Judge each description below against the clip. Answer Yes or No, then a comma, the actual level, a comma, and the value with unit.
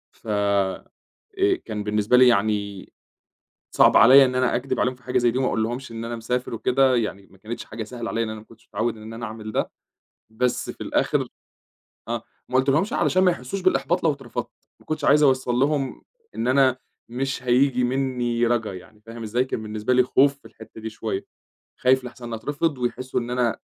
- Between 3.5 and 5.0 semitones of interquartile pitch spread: No, average, 2.8 semitones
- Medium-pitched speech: No, low, 120 Hz